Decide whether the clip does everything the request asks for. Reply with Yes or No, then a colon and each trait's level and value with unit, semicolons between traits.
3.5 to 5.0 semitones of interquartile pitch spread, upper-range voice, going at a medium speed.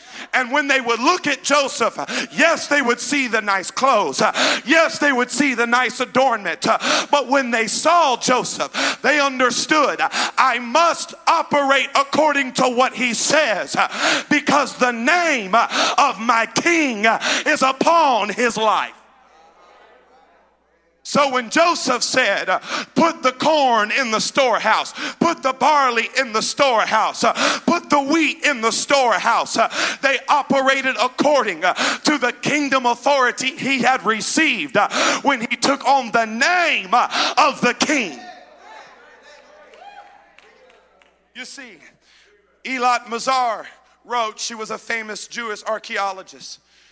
No: average, 4.0 semitones; very high, 265 Hz; slow, 125 wpm